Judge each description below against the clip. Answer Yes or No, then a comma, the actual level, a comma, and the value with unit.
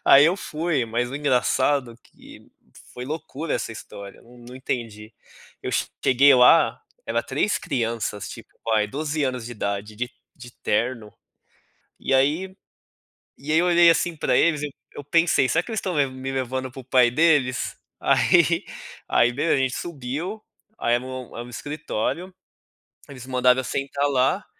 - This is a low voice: Yes, low, 130 Hz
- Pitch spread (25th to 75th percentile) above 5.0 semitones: No, average, 3.9 semitones